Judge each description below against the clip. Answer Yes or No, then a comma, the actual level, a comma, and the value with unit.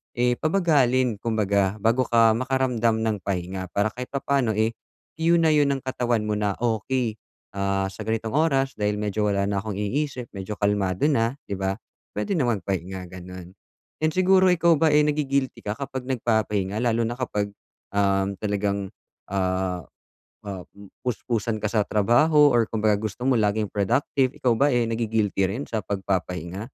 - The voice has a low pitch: Yes, low, 110 Hz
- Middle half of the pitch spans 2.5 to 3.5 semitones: No, average, 4.3 semitones